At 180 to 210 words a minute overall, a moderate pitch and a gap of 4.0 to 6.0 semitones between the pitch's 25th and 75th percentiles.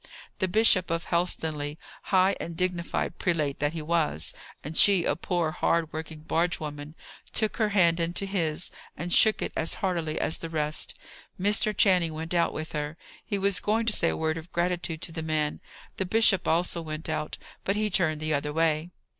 No: average, 190 wpm; medium, 165 Hz; average, 2.8 semitones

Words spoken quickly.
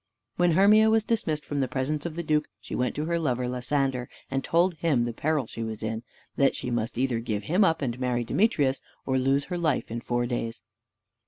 Yes: fast, 225 wpm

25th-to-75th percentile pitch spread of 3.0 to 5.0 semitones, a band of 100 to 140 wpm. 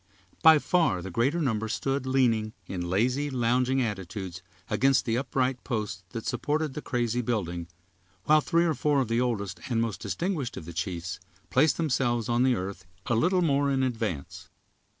No: average, 4.7 semitones; average, 170 wpm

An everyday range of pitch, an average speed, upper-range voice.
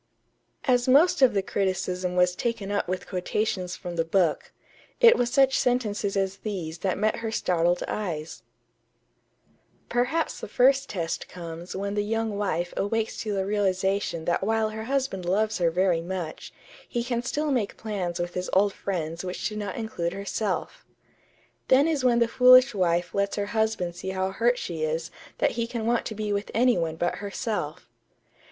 Yes: average, 4.3 semitones; average, 180 wpm; high, 200 Hz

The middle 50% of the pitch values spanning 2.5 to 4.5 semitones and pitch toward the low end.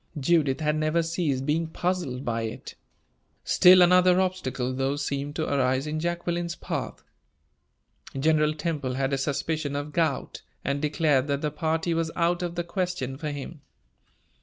No: average, 3.6 semitones; medium, 155 Hz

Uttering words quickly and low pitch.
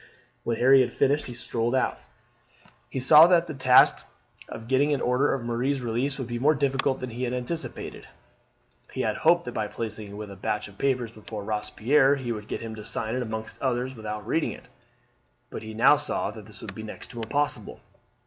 Yes: fast, 210 wpm; low, 120 Hz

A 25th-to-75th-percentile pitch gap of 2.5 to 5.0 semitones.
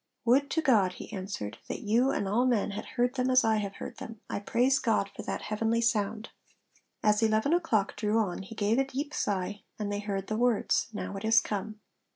Yes: average, 3.0 semitones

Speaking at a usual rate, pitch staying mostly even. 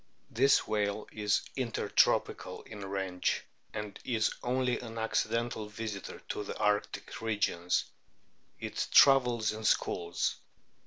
No: slow, 110 wpm; narrow, 2.3 semitones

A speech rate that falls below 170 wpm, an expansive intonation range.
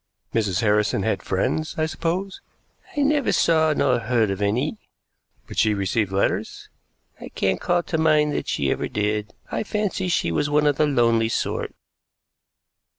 Yes: average, 160 wpm; wide, 7.4 semitones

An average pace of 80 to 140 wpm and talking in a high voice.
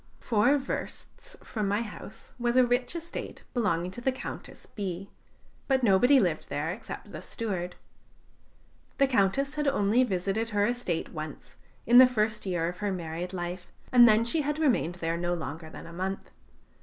No: average, 170 wpm; high, 210 Hz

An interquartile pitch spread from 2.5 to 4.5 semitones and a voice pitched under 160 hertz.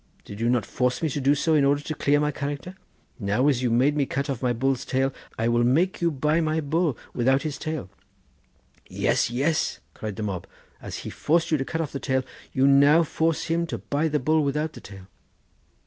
Yes: average, 3.6 semitones; medium, 140 Hz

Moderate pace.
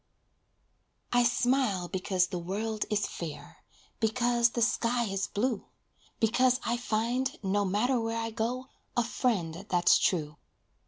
No: slow, 130 wpm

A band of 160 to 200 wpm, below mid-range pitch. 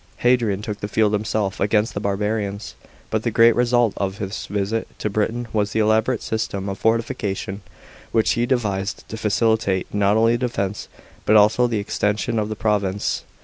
Yes: average, 180 wpm; low, 105 Hz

